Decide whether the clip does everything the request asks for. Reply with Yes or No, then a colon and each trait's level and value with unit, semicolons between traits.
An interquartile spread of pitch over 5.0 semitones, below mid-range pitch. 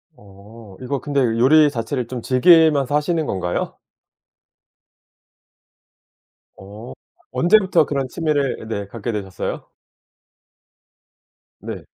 Yes: wide, 5.4 semitones; low, 125 Hz